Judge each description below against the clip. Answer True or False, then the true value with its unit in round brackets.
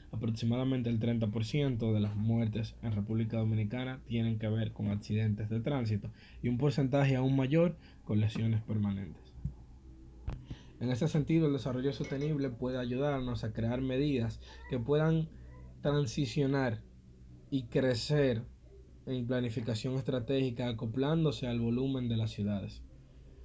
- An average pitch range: True (3.7 semitones)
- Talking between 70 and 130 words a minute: True (125 wpm)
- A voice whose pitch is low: True (120 Hz)